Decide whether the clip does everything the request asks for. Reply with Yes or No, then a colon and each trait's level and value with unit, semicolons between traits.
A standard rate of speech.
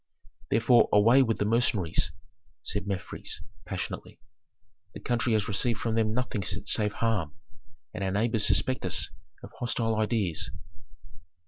No: slow, 130 wpm